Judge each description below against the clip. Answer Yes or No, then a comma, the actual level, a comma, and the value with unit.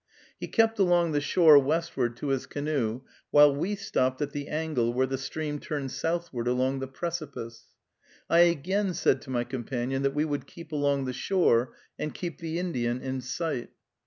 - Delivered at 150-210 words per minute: Yes, average, 180 wpm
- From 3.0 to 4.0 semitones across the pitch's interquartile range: No, average, 4.4 semitones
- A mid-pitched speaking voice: Yes, medium, 145 Hz